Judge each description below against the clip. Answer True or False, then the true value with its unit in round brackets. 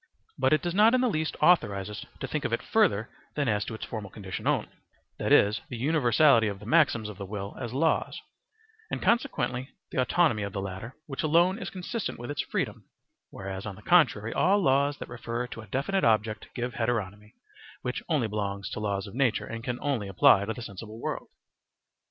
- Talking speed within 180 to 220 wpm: True (205 wpm)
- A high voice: False (120 Hz)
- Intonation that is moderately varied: False (6.3 semitones)